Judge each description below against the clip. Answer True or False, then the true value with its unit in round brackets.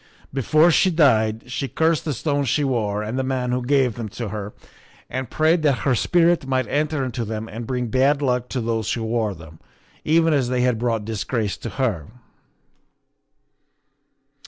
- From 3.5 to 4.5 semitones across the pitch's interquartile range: True (4.1 semitones)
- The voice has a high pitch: False (125 Hz)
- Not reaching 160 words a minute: False (180 wpm)